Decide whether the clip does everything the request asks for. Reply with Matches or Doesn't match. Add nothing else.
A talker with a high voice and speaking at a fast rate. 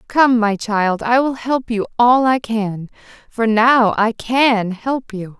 Doesn't match